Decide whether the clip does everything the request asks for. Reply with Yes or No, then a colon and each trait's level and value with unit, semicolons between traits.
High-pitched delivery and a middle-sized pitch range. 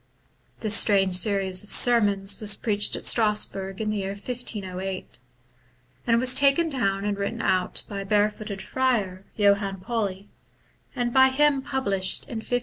Yes: high, 210 Hz; average, 3.5 semitones